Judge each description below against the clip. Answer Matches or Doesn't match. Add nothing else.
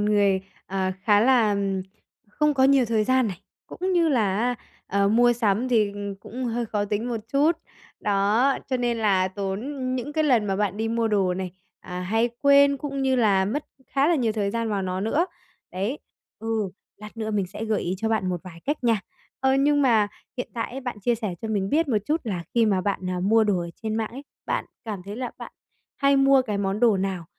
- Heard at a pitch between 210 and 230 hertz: Matches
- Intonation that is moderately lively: Matches